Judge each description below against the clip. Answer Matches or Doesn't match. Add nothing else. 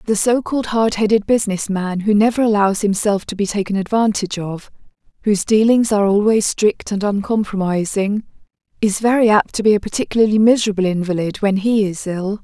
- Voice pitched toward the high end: Matches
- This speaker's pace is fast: Doesn't match